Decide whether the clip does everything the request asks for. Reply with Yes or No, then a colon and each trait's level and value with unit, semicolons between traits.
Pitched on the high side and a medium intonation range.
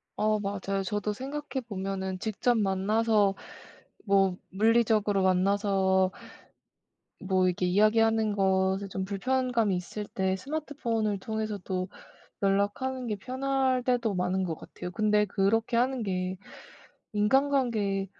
Yes: high, 205 Hz; average, 3.1 semitones